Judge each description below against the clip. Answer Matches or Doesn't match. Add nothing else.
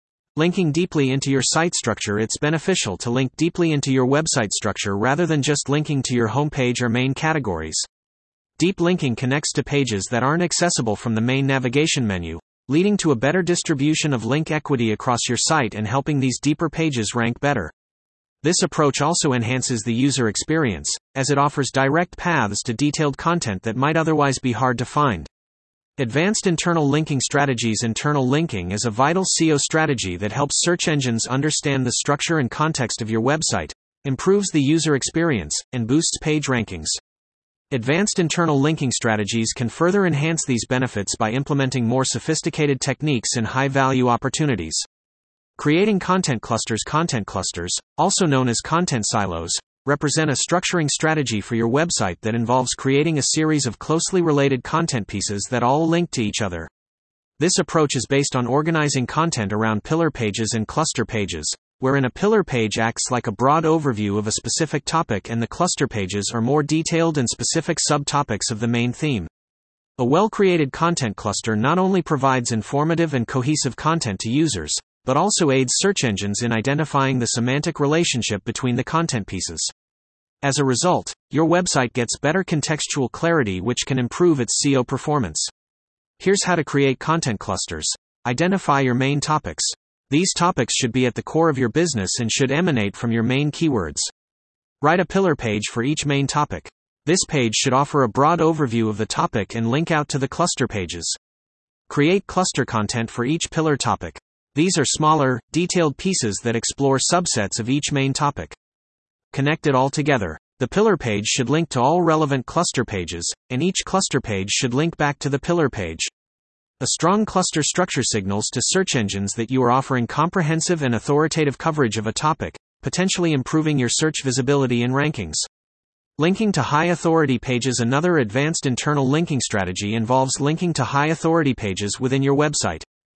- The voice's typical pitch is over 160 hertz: Doesn't match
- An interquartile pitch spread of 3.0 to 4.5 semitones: Doesn't match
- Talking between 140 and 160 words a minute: Doesn't match